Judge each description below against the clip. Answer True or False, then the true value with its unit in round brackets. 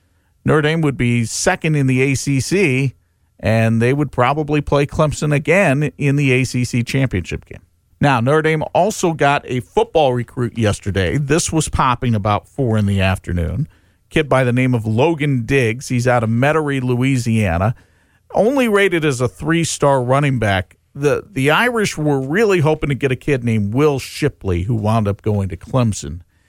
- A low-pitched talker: True (130 Hz)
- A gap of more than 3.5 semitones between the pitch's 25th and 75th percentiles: True (5.2 semitones)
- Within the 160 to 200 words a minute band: True (170 wpm)